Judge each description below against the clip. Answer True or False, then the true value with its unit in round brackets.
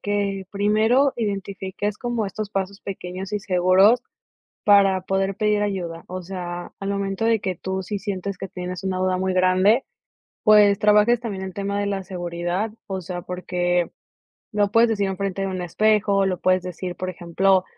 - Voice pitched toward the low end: False (195 Hz)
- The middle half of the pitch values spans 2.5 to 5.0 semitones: False (1.9 semitones)